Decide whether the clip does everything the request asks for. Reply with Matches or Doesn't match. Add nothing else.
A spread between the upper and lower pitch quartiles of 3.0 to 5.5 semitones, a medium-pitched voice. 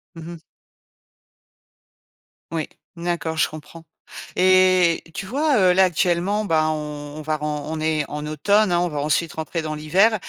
Matches